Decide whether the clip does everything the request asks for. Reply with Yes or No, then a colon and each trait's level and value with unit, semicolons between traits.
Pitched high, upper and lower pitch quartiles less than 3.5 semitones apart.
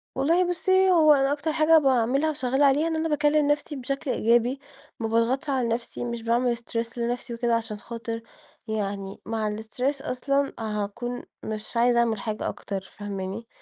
No: high, 240 Hz; average, 3.8 semitones